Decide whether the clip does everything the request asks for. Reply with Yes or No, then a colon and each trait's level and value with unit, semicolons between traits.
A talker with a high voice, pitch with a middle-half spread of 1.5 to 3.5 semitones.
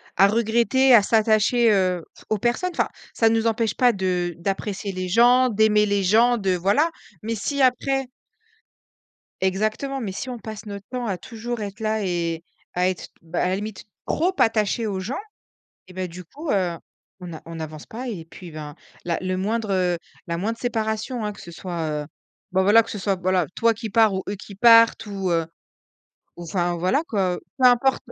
No: high, 205 Hz; average, 3.9 semitones